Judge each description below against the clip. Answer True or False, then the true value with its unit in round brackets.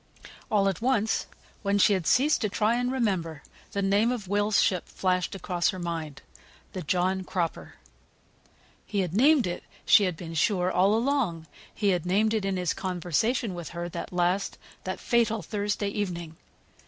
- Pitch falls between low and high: False (195 Hz)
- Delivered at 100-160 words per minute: False (170 wpm)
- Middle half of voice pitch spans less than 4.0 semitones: True (3.3 semitones)